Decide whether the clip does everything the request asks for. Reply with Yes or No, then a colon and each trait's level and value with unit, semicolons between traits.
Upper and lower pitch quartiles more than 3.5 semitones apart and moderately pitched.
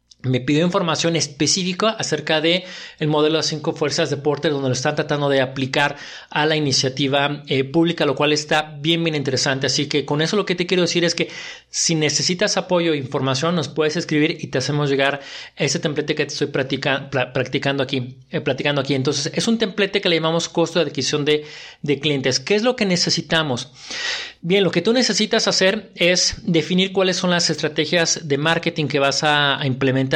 No: average, 3.1 semitones; medium, 155 Hz